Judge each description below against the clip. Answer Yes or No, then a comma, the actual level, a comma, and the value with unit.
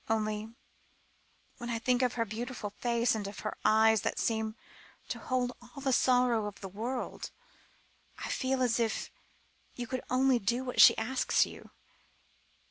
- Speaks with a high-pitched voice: Yes, high, 235 Hz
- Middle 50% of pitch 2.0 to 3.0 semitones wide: Yes, narrow, 2.4 semitones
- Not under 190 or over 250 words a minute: No, average, 160 wpm